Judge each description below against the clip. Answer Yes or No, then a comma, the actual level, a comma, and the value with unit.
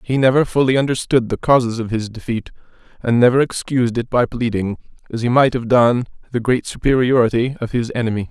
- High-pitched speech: No, low, 120 Hz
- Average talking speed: Yes, average, 190 wpm